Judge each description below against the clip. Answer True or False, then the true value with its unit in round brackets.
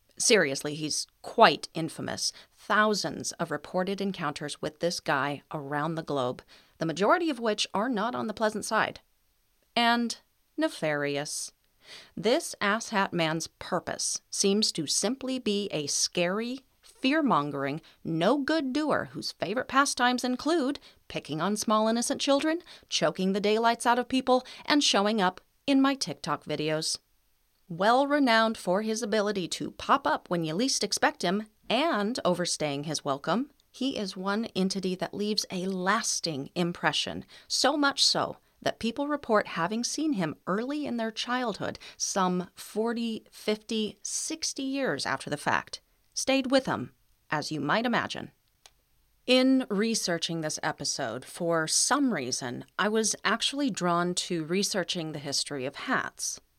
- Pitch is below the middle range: False (205 Hz)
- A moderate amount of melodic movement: False (7.5 semitones)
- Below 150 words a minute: True (140 wpm)